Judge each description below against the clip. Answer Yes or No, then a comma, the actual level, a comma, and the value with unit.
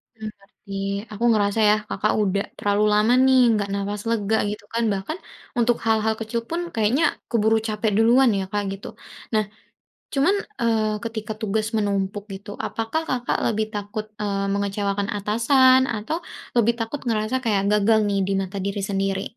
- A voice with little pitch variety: Yes, narrow, 2.2 semitones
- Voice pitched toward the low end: No, high, 215 Hz